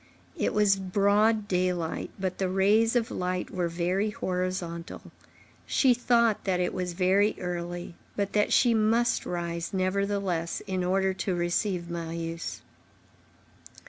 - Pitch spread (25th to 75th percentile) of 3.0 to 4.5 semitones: No, narrow, 2.6 semitones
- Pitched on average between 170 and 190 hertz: Yes, medium, 185 Hz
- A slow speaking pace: Yes, slow, 130 wpm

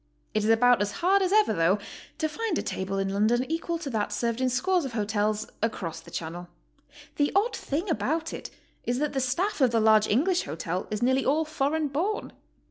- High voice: Yes, very high, 255 Hz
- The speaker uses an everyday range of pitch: No, wide, 7.2 semitones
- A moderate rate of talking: No, fast, 210 wpm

